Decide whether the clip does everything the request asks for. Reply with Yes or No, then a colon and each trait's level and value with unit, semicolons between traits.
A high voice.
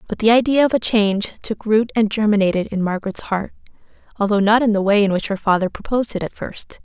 Yes: high, 210 Hz